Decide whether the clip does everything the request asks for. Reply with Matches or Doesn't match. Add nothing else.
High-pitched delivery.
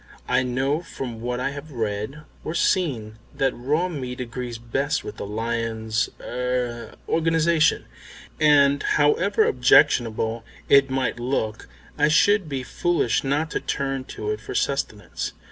Doesn't match